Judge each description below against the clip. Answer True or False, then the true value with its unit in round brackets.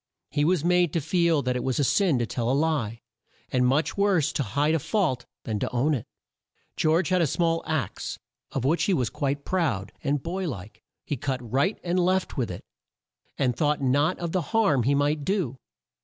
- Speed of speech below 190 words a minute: False (205 wpm)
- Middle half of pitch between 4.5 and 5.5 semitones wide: True (5.1 semitones)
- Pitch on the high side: False (145 Hz)